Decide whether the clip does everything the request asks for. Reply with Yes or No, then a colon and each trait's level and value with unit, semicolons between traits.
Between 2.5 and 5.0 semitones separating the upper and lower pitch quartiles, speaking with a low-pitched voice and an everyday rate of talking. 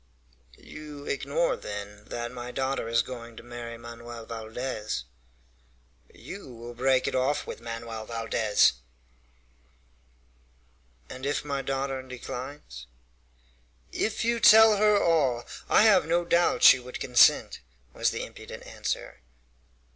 No: average, 3.9 semitones; low, 125 Hz; slow, 125 wpm